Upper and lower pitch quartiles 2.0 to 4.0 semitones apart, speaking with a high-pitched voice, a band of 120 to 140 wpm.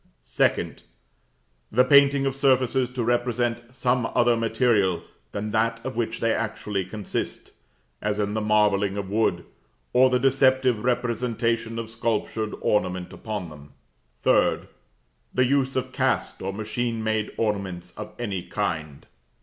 No: average, 3.1 semitones; low, 115 Hz; slow, 135 wpm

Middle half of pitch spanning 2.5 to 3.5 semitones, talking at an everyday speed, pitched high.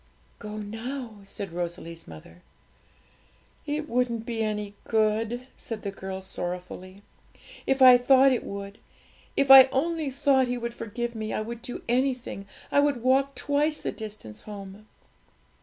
No: average, 4.6 semitones; average, 145 wpm; high, 230 Hz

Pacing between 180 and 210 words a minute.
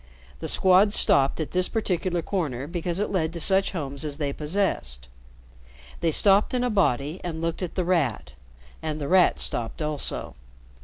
No: average, 170 wpm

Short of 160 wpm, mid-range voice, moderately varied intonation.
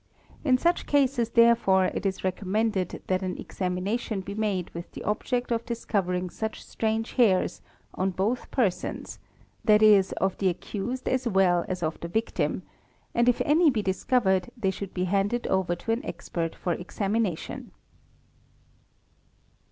No: average, 150 wpm; high, 200 Hz; average, 4.0 semitones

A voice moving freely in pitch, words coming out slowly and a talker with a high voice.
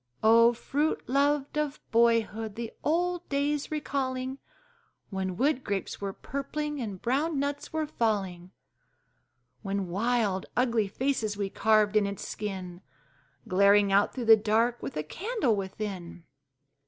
Yes: wide, 5.8 semitones; slow, 130 wpm; high, 230 Hz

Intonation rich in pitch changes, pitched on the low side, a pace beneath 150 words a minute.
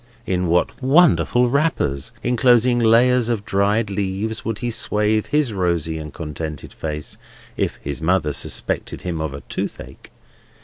Yes: wide, 6.9 semitones; low, 100 Hz; average, 140 wpm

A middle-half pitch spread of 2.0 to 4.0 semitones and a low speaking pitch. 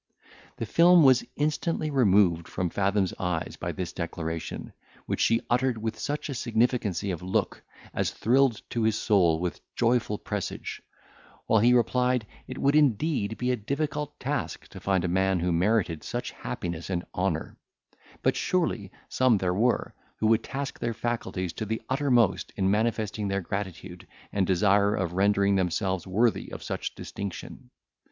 No: average, 4.9 semitones; low, 105 Hz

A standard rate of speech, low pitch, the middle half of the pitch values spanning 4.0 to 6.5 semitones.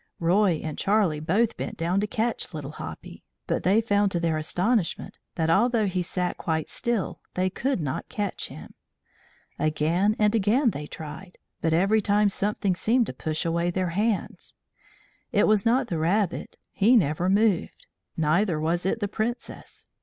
No: average, 165 wpm; high, 190 Hz; average, 4.5 semitones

